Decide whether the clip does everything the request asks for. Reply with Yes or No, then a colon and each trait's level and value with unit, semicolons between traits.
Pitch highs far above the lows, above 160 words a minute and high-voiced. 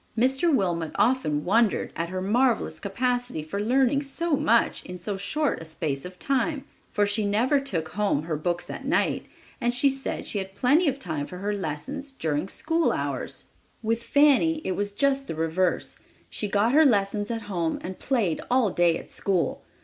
Yes: wide, 6.8 semitones; average, 185 wpm; high, 210 Hz